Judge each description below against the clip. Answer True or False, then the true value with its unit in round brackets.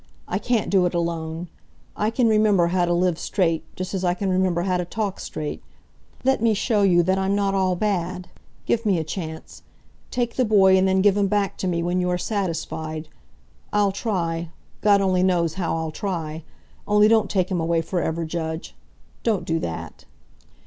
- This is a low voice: False (185 Hz)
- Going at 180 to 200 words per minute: True (190 wpm)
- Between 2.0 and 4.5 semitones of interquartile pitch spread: True (3.1 semitones)